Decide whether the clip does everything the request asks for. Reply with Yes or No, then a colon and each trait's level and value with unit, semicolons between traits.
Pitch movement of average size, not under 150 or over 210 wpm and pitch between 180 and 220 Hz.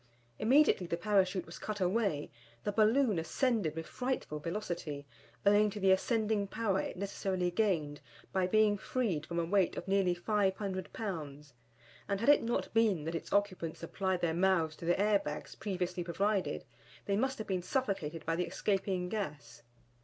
Yes: average, 3.7 semitones; average, 170 wpm; high, 190 Hz